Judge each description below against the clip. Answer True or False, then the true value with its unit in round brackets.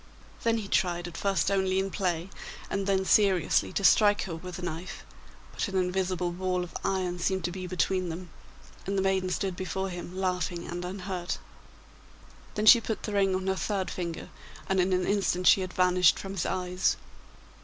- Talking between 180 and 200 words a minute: True (190 wpm)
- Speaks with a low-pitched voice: False (185 Hz)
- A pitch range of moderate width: False (1.3 semitones)